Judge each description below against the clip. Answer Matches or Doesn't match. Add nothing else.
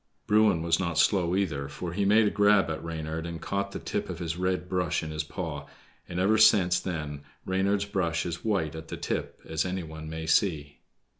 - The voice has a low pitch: Matches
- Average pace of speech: Doesn't match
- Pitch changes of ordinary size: Matches